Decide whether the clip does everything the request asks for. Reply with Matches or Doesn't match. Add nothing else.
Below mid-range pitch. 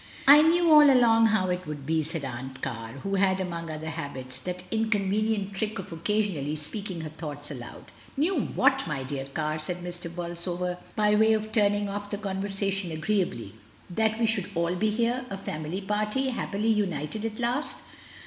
Doesn't match